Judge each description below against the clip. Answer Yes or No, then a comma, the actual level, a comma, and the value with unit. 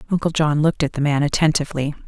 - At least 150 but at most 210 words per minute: Yes, fast, 205 wpm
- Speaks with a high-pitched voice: No, medium, 150 Hz